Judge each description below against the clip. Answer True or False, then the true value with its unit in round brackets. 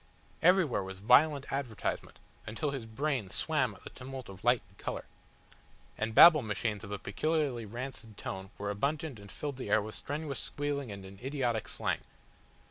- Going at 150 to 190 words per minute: True (170 wpm)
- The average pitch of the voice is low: True (120 Hz)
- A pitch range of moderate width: False (5.7 semitones)